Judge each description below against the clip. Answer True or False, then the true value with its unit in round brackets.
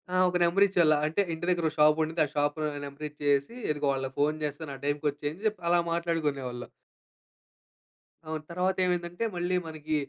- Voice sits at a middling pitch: True (155 Hz)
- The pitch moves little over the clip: False (3.0 semitones)